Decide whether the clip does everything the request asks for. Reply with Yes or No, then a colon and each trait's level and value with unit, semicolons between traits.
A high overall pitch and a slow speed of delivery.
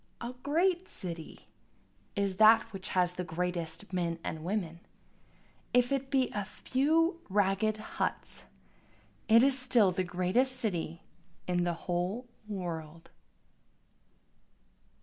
Yes: high, 195 Hz; slow, 115 wpm